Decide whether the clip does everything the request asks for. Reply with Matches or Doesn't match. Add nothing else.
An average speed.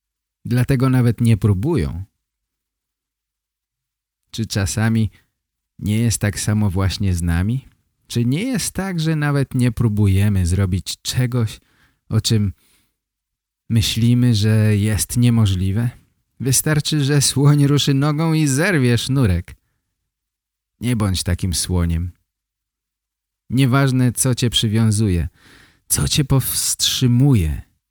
Doesn't match